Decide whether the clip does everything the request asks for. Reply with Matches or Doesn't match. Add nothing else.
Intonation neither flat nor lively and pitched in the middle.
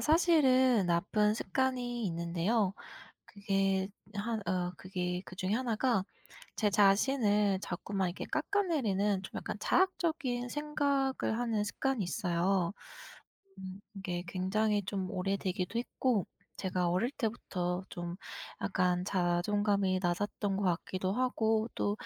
Doesn't match